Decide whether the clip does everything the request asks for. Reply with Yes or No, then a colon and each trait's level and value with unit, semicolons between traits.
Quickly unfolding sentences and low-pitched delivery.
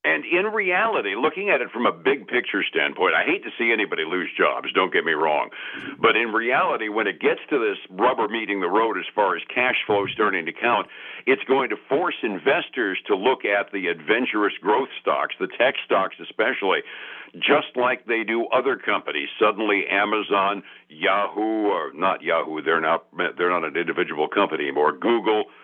No: average, 180 wpm; low, 120 Hz